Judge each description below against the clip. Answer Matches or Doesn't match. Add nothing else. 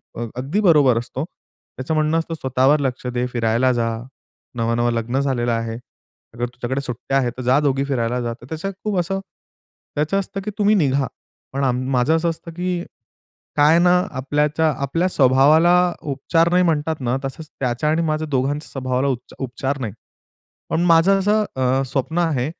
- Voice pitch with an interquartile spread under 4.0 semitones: Doesn't match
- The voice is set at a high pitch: Doesn't match